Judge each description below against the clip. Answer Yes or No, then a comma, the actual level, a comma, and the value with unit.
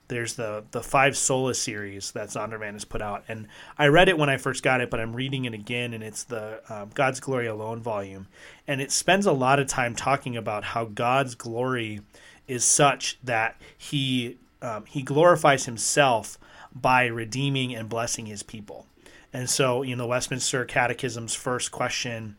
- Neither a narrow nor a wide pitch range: Yes, average, 3.1 semitones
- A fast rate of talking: No, average, 185 wpm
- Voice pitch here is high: No, low, 125 Hz